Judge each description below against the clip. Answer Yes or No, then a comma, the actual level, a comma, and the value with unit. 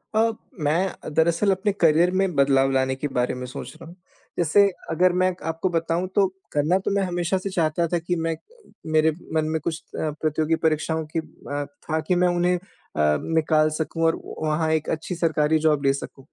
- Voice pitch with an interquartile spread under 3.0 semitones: Yes, narrow, 2.4 semitones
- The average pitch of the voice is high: No, medium, 160 Hz